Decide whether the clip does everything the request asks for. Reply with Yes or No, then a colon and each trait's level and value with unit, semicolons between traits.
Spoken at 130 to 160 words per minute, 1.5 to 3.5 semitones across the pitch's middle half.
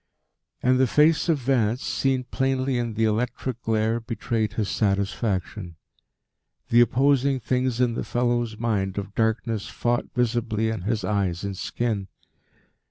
Yes: average, 140 wpm; average, 2.9 semitones